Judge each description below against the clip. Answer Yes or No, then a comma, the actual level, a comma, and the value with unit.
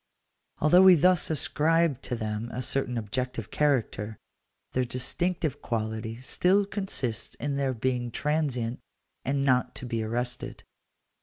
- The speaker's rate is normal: No, slow, 130 wpm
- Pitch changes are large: No, average, 4.6 semitones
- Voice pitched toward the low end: Yes, low, 130 Hz